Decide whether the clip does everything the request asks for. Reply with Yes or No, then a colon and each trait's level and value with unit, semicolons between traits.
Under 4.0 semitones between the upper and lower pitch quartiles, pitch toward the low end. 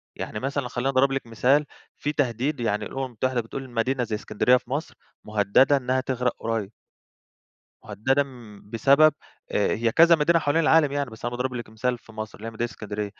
Yes: average, 3.4 semitones; low, 125 Hz